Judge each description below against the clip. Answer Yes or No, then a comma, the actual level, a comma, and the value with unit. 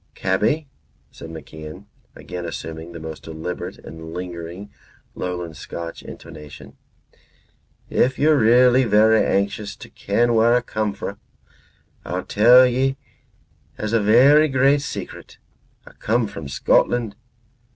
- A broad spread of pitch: Yes, wide, 6.5 semitones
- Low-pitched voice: Yes, low, 105 Hz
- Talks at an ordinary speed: No, slow, 120 wpm